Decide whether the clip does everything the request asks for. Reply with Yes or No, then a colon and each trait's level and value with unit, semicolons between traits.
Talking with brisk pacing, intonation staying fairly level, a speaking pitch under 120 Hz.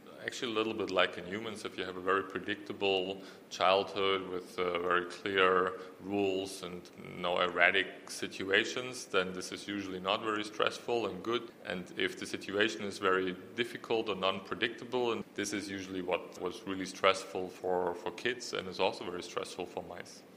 No: average, 175 wpm; narrow, 1.5 semitones; very low, 95 Hz